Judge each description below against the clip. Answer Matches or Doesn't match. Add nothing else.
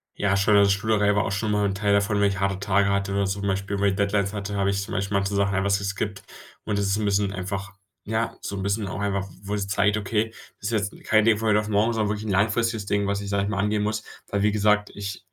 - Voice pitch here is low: Matches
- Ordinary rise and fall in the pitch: Doesn't match